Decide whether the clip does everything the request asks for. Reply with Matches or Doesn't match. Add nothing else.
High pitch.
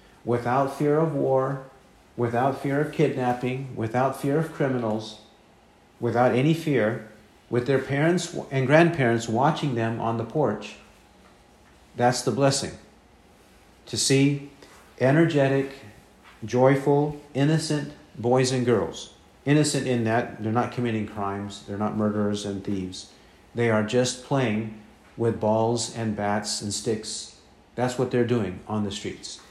Doesn't match